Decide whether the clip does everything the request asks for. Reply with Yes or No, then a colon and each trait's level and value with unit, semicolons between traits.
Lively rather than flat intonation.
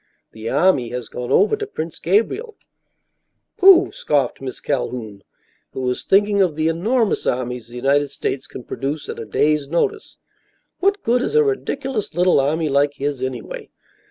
Yes: wide, 8.3 semitones